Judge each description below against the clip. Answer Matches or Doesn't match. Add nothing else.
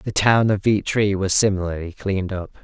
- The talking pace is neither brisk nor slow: Matches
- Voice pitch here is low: Matches